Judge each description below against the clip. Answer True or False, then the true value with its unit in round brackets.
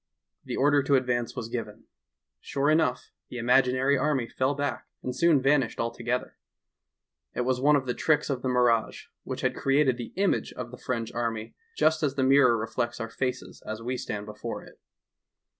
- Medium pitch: False (125 Hz)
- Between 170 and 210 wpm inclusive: True (185 wpm)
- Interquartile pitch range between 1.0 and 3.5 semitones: True (2.9 semitones)